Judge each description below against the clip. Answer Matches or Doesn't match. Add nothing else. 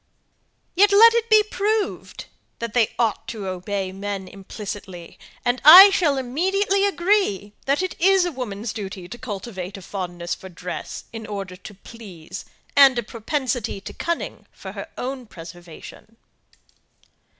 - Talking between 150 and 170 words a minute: Doesn't match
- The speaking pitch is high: Matches